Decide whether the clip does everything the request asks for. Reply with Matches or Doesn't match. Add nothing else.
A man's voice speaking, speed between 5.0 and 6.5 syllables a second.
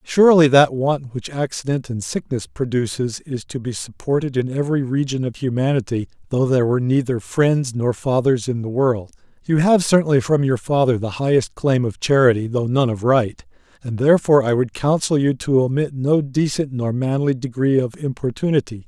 Matches